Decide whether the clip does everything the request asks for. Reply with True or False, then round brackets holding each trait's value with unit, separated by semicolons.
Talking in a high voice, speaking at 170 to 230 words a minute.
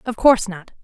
True (215 Hz; 215 wpm)